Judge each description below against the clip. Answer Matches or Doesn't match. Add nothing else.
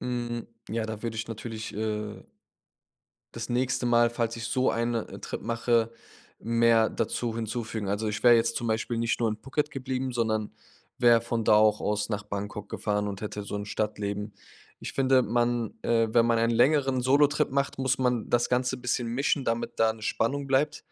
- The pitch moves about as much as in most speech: Doesn't match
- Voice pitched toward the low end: Matches